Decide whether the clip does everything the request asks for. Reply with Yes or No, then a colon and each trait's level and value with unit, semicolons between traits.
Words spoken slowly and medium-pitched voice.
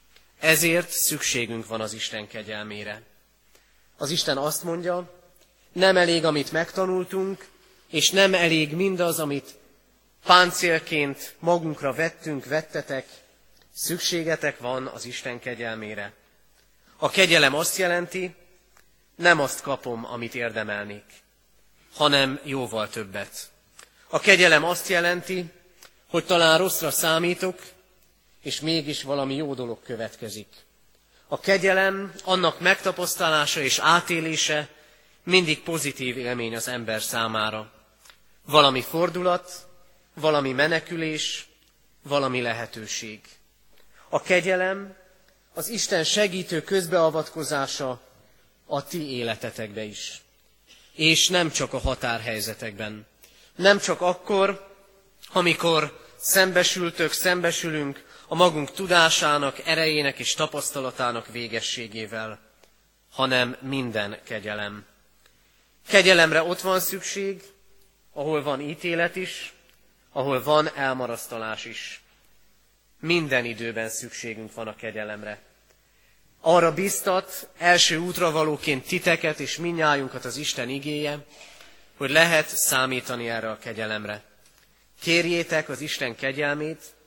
Yes: slow, 100 wpm; medium, 150 Hz